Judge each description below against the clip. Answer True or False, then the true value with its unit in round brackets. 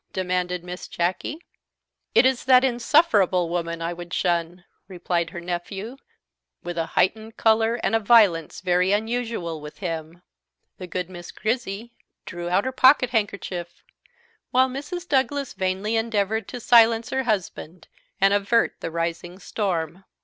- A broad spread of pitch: False (4.8 semitones)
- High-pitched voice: True (195 Hz)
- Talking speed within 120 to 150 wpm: True (140 wpm)